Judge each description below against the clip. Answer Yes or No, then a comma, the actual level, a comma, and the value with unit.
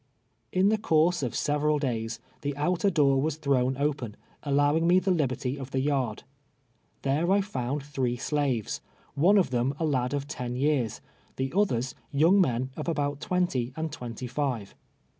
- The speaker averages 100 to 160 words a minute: No, average, 170 wpm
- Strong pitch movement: No, average, 3.8 semitones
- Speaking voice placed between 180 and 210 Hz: No, medium, 140 Hz